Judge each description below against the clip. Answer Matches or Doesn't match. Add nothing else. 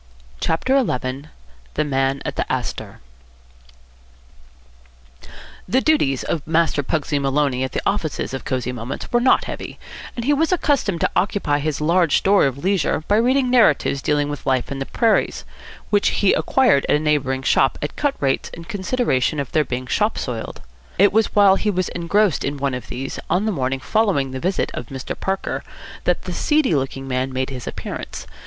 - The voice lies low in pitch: Doesn't match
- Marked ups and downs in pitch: Matches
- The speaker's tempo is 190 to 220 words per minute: Doesn't match